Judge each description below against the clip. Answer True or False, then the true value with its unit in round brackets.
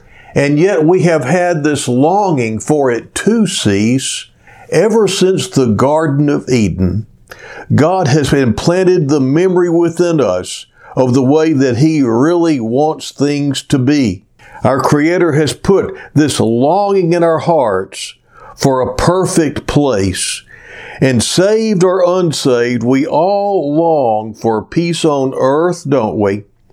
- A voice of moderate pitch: True (150 Hz)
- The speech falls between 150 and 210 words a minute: False (135 wpm)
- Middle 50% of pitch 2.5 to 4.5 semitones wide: False (5.6 semitones)